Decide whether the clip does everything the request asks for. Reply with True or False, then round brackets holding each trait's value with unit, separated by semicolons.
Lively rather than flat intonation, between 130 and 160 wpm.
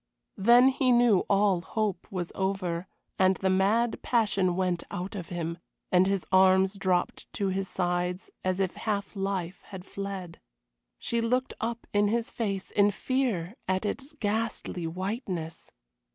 False (3.0 semitones; 150 wpm)